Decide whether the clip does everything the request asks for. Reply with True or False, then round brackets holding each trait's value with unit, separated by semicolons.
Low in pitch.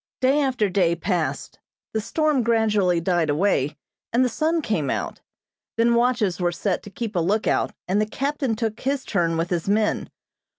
False (210 Hz)